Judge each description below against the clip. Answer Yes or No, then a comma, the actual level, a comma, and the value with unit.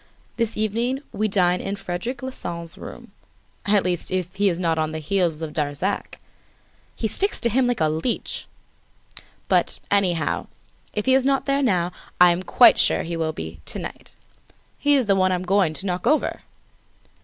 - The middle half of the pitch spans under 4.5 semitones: No, wide, 5.4 semitones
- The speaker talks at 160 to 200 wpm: Yes, average, 180 wpm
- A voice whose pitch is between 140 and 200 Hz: Yes, high, 190 Hz